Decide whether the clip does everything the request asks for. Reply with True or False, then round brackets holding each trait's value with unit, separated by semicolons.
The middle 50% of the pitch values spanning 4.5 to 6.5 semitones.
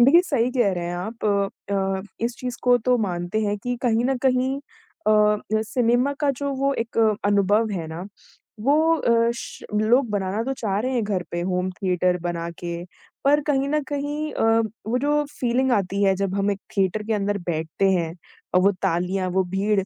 True (4.9 semitones)